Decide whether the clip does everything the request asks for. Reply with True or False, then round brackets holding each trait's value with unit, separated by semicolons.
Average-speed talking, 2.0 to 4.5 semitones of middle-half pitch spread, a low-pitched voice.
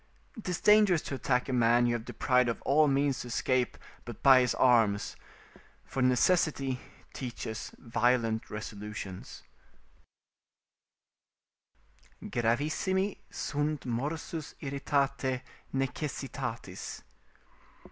False (95 wpm; 3.5 semitones; 130 Hz)